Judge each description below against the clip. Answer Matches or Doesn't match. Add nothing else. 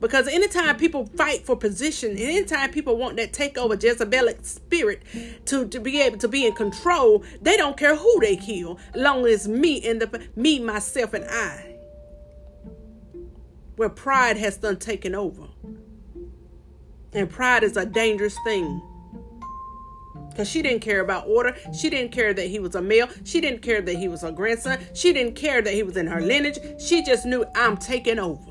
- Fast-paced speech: Doesn't match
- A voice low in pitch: Doesn't match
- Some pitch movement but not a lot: Doesn't match